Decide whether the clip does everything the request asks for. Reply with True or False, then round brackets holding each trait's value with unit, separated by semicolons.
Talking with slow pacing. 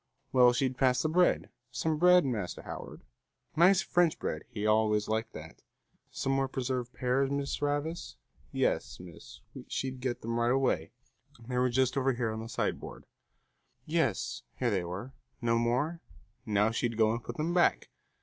False (165 wpm)